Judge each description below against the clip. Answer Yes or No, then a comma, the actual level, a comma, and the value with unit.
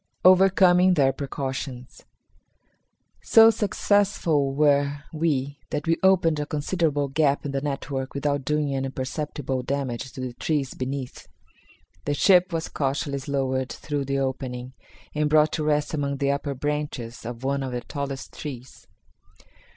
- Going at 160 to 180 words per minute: No, average, 145 wpm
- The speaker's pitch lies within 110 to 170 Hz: Yes, medium, 140 Hz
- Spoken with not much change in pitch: Yes, narrow, 2.2 semitones